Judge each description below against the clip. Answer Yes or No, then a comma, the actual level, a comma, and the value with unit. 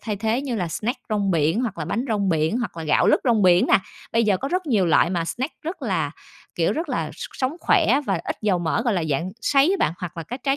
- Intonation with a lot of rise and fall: Yes, wide, 6.3 semitones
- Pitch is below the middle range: No, high, 210 Hz